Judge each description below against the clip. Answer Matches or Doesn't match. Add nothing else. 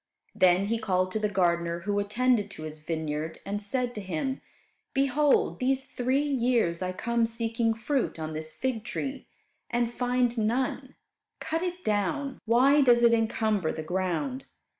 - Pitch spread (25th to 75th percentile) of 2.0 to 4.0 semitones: Doesn't match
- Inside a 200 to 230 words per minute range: Doesn't match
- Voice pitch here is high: Matches